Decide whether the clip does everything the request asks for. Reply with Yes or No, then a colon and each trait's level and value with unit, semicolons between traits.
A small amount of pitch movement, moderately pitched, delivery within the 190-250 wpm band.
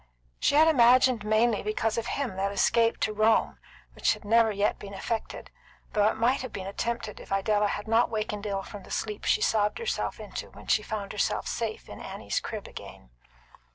No: narrow, 2.1 semitones; high, 215 Hz; average, 195 wpm